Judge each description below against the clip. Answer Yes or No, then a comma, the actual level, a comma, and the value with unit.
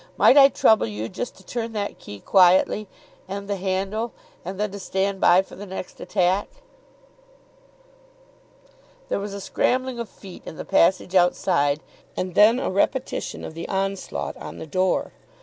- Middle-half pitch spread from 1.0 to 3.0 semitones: Yes, narrow, 2.5 semitones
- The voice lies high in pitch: Yes, high, 195 Hz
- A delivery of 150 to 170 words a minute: Yes, average, 165 wpm